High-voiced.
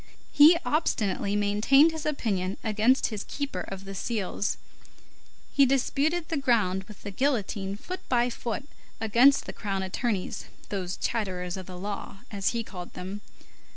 Yes: high, 210 Hz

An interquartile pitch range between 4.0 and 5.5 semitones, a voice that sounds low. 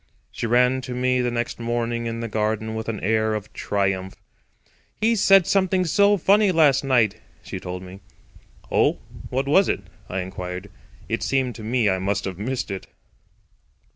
Yes: average, 4.7 semitones; low, 115 Hz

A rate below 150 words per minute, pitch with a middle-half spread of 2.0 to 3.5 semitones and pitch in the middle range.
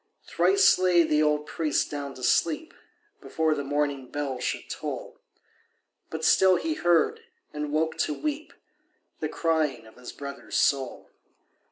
Yes: average, 140 wpm; average, 3.0 semitones; medium, 150 Hz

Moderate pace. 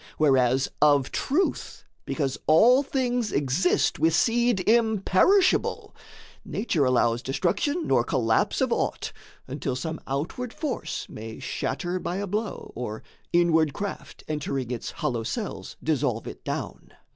No: slow, 125 wpm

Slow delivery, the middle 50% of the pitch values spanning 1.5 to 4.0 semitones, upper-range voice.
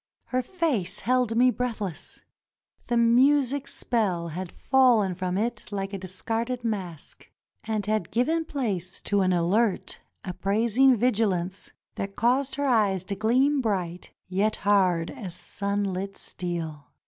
No: slow, 130 wpm; average, 4.9 semitones; high, 210 Hz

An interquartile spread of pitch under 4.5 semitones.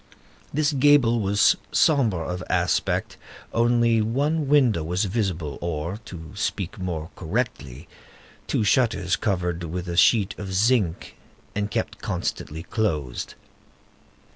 No: wide, 5.4 semitones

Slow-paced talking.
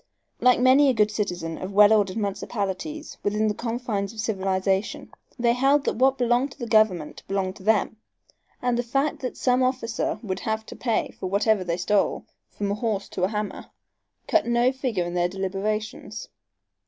No: average, 180 wpm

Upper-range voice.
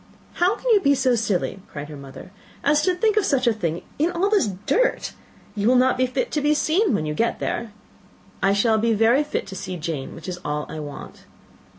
Yes: high, 230 Hz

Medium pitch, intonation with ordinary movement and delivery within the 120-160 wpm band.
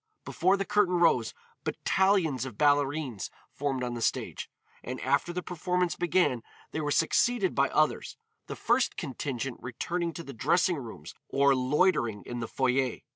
No: medium, 145 Hz; wide, 5.7 semitones; average, 155 wpm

